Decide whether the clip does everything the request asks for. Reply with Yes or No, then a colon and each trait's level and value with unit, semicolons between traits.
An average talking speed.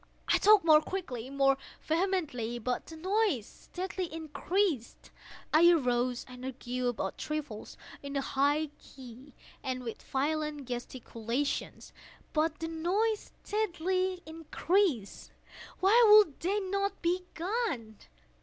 No: slow, 115 wpm